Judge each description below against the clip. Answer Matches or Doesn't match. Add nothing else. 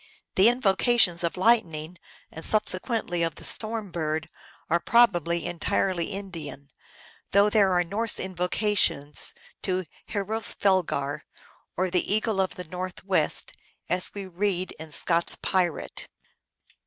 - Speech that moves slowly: Matches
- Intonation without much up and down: Doesn't match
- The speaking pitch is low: Doesn't match